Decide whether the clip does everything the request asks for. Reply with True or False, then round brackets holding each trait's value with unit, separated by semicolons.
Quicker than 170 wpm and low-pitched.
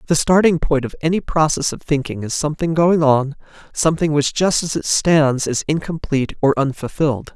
False (180 wpm; 150 Hz)